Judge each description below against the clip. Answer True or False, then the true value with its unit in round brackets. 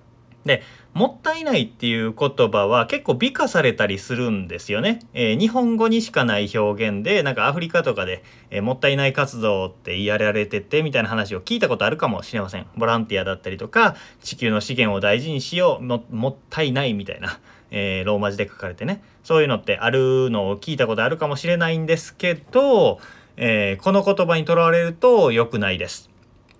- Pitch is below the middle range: True (130 Hz)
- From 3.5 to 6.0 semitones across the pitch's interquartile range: False (8.2 semitones)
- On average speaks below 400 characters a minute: False (415 characters per minute)